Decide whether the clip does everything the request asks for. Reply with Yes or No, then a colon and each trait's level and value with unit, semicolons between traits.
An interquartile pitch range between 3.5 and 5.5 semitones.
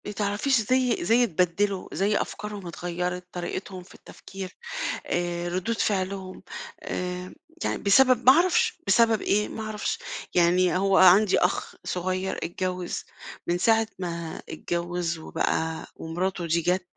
No: average, 2.9 semitones